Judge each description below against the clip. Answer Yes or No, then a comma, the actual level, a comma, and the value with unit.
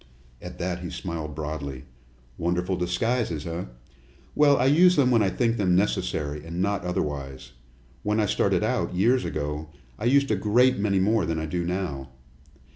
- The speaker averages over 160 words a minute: Yes, average, 170 wpm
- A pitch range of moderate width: No, wide, 6.1 semitones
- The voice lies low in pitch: Yes, very low, 90 Hz